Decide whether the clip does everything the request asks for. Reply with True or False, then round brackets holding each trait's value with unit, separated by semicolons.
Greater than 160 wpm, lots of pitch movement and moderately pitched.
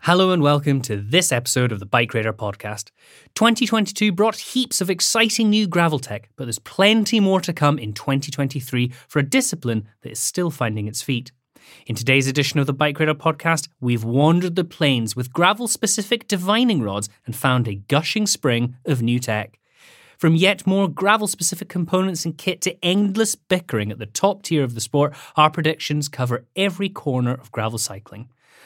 True (180 wpm; 7.5 semitones; 150 Hz)